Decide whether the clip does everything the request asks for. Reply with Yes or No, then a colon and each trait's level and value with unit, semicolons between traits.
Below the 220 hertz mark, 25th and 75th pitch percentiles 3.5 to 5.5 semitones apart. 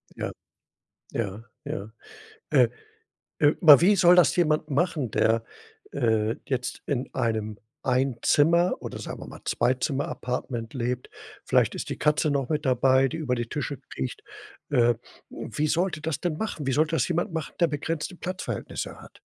Yes: medium, 140 Hz; average, 4.8 semitones